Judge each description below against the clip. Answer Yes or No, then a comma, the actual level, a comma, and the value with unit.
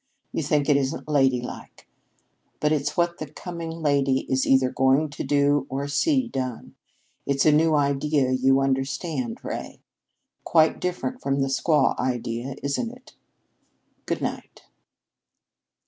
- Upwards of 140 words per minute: No, slow, 135 wpm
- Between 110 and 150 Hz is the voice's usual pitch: Yes, medium, 140 Hz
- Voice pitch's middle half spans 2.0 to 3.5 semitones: Yes, average, 2.7 semitones